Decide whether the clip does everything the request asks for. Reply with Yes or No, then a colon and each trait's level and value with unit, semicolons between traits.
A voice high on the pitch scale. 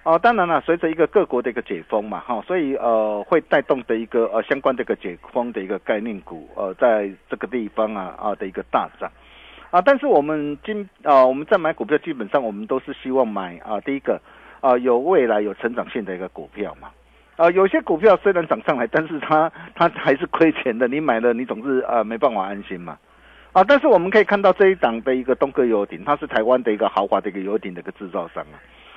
No: medium, 140 Hz